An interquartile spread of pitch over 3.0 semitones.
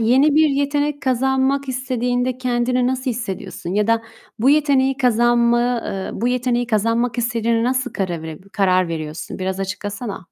Yes: average, 3.7 semitones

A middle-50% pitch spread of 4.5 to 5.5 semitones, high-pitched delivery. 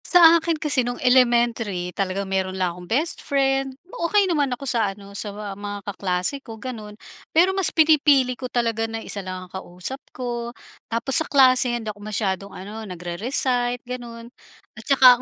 Yes: average, 5.0 semitones; high, 235 Hz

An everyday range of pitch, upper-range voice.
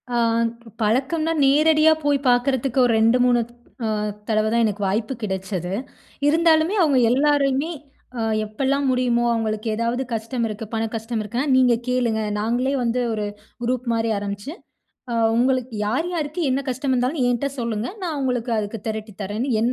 Yes: average, 3.6 semitones; high, 245 Hz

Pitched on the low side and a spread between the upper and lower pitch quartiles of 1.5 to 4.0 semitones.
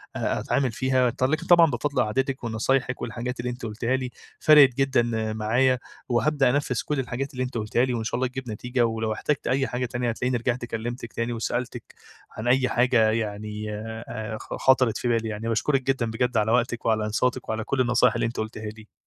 Yes: low, 120 Hz; narrow, 2.5 semitones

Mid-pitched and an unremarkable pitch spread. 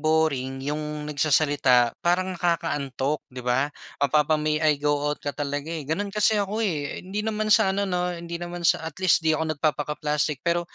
Yes: medium, 155 Hz; average, 3.4 semitones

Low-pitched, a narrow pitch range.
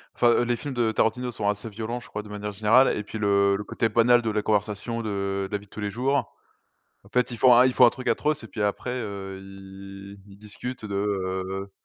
No: low, 105 Hz; average, 3.1 semitones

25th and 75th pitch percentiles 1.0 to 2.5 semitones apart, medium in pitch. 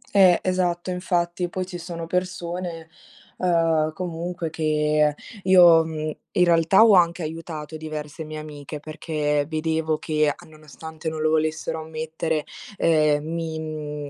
Yes: narrow, 2.0 semitones; medium, 160 Hz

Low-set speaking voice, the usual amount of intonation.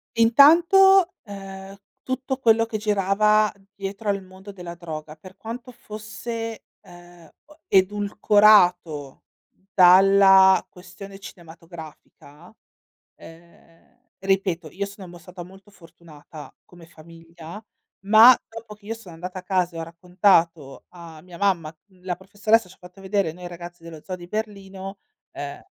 No: high, 190 Hz; average, 3.4 semitones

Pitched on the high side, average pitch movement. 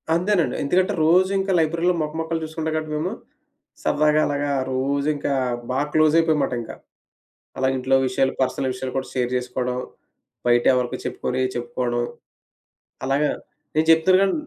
No: medium, 145 Hz; average, 4.0 semitones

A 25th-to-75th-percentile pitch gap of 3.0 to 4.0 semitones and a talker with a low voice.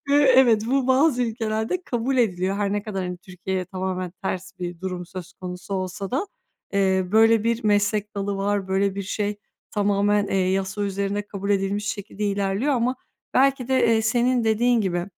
No: average, 3.3 semitones; high, 205 Hz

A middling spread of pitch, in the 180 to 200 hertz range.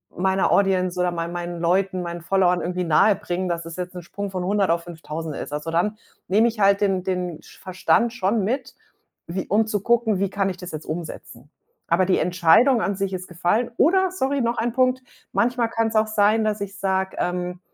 Yes: average, 3.5 semitones; high, 190 Hz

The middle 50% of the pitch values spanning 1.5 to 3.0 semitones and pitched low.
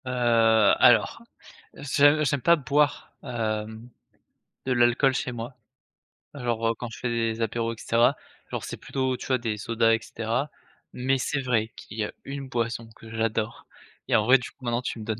Yes: narrow, 2.5 semitones; low, 120 Hz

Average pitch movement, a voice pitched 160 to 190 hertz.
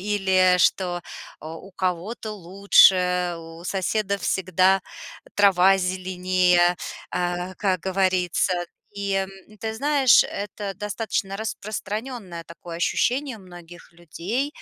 No: narrow, 2.3 semitones; medium, 185 Hz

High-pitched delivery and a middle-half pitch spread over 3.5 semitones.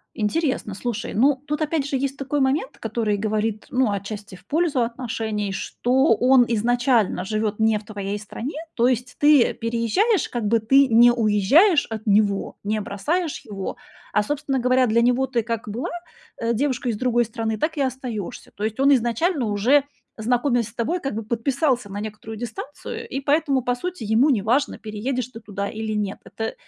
Yes: high, 235 Hz; average, 3.9 semitones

